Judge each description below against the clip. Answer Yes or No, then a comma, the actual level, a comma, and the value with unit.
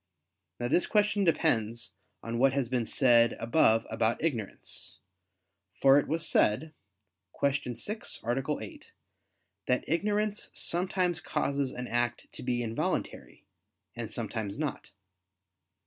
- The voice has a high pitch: No, low, 130 Hz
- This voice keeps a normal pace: No, slow, 120 wpm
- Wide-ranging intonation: Yes, wide, 5.7 semitones